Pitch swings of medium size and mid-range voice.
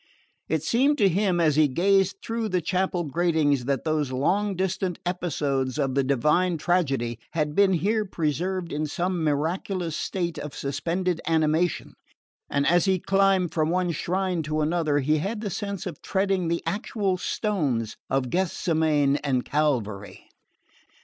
Yes: average, 4.2 semitones; medium, 170 Hz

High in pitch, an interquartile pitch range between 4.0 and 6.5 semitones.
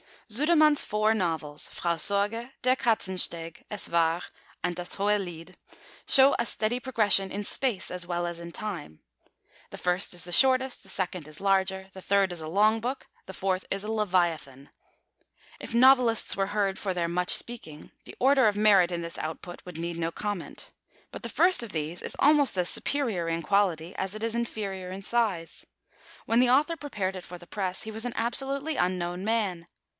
Yes: high, 195 Hz; average, 4.6 semitones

